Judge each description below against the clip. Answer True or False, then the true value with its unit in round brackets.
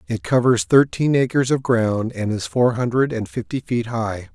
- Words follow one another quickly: False (195 wpm)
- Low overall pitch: True (120 Hz)